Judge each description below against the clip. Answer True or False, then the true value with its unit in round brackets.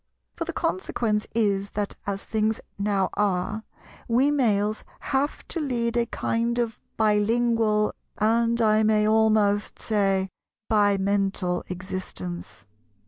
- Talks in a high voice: True (215 Hz)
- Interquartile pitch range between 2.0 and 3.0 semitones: True (2.5 semitones)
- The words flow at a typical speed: False (120 wpm)